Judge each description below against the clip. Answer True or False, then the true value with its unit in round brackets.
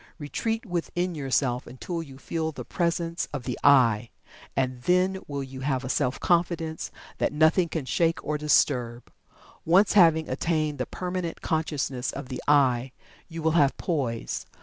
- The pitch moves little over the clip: False (4.3 semitones)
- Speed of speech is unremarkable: True (155 wpm)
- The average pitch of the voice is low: False (150 Hz)